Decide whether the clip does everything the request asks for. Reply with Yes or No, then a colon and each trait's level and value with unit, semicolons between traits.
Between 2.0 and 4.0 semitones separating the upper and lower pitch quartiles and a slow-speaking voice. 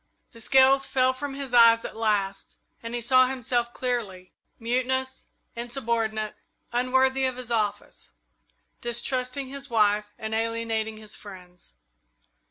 Yes: average, 2.9 semitones; slow, 125 wpm